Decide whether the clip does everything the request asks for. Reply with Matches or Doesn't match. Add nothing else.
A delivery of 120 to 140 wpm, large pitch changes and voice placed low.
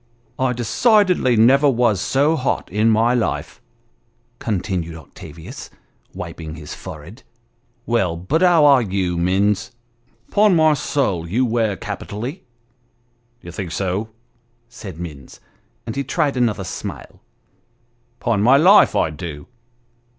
Matches